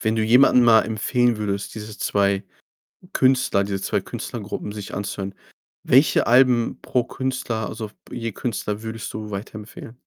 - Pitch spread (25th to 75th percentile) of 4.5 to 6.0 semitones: No, average, 2.7 semitones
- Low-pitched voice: Yes, low, 110 Hz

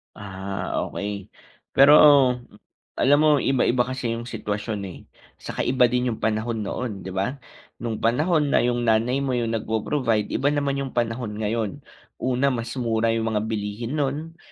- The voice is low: Yes, low, 115 Hz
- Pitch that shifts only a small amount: No, average, 3.3 semitones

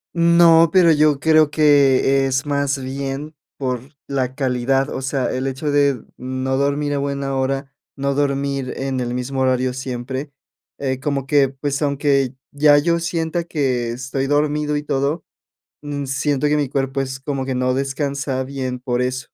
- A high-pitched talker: No, medium, 140 Hz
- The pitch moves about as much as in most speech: No, narrow, 1.8 semitones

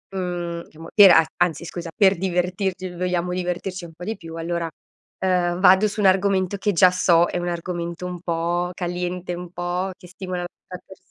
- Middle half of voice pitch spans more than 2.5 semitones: No, narrow, 1.3 semitones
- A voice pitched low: No, medium, 180 Hz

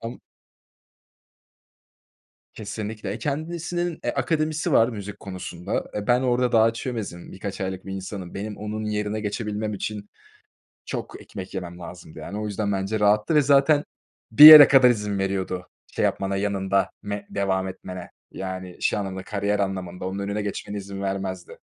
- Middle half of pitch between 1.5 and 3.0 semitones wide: Yes, average, 2.7 semitones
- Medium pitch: No, low, 100 Hz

